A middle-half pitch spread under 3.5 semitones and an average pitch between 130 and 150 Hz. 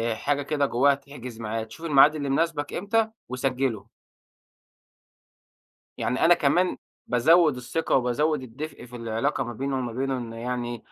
No: average, 3.8 semitones; low, 135 Hz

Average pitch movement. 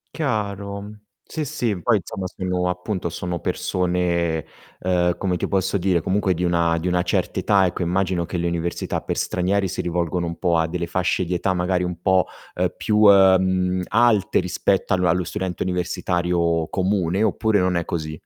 No: narrow, 1.8 semitones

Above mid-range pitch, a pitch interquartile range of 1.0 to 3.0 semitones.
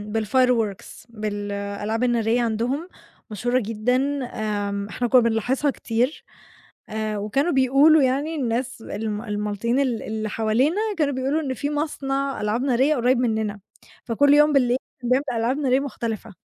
No: high, 245 Hz; average, 3.8 semitones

